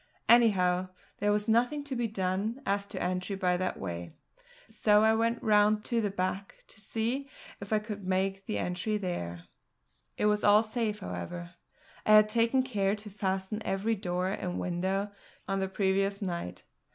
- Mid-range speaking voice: No, high, 200 Hz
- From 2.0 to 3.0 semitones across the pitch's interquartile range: Yes, average, 2.7 semitones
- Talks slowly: No, average, 170 wpm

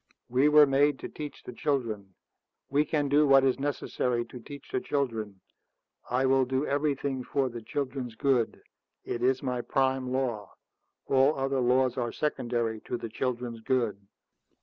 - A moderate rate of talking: Yes, average, 160 wpm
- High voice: No, low, 130 Hz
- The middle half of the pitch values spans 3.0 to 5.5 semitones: No, narrow, 2.6 semitones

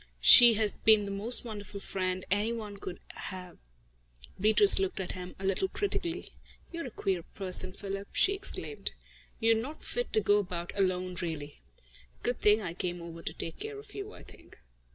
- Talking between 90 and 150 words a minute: No, average, 180 wpm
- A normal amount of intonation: Yes, average, 3.9 semitones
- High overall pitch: Yes, high, 200 Hz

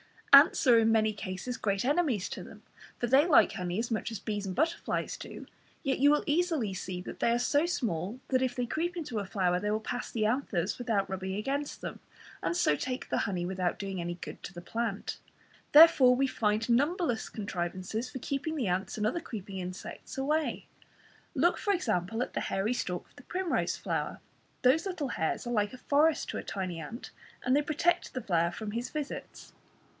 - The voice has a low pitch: No, high, 235 Hz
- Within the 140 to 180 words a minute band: No, average, 200 wpm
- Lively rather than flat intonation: Yes, wide, 6.5 semitones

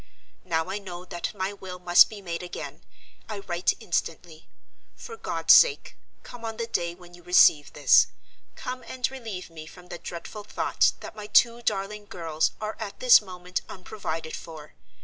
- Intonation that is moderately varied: Yes, average, 3.7 semitones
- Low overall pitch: No, medium, 185 Hz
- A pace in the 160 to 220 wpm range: Yes, average, 170 wpm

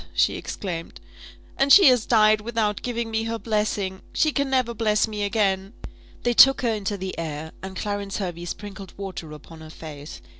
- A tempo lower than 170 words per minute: No, average, 180 wpm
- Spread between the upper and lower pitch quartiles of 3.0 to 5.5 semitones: Yes, average, 3.4 semitones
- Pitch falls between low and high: No, high, 205 Hz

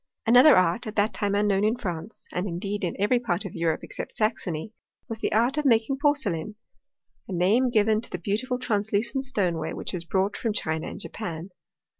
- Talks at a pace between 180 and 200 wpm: Yes, average, 190 wpm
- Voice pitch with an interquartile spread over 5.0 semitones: No, average, 4.3 semitones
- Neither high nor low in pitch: No, high, 205 Hz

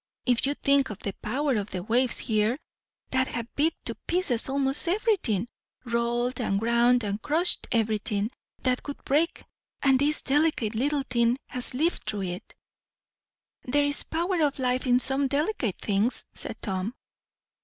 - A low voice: No, very high, 250 Hz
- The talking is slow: No, average, 160 wpm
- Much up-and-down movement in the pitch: No, average, 4.3 semitones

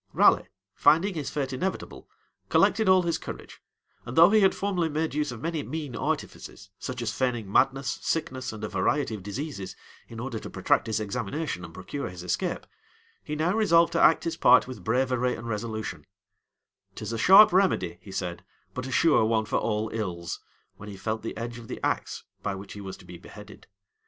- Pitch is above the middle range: No, low, 125 Hz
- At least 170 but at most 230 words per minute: Yes, average, 195 wpm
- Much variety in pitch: Yes, wide, 6.8 semitones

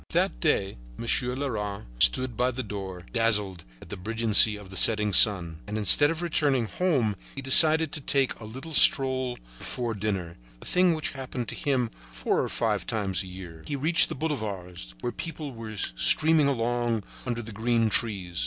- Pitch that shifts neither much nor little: Yes, average, 5.0 semitones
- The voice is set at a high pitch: No, low, 115 Hz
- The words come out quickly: No, average, 180 wpm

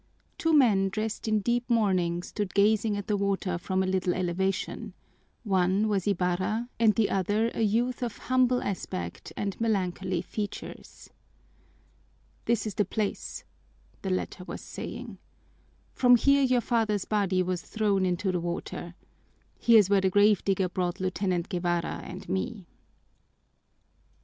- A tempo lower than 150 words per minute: Yes, average, 140 wpm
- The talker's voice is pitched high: Yes, high, 200 Hz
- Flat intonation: No, average, 3.0 semitones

